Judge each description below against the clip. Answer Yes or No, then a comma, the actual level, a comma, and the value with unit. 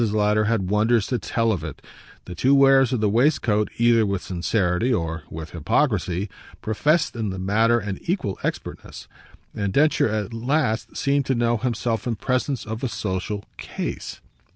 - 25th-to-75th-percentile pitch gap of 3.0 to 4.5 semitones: Yes, average, 3.6 semitones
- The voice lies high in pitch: No, low, 110 Hz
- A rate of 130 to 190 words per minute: Yes, average, 165 wpm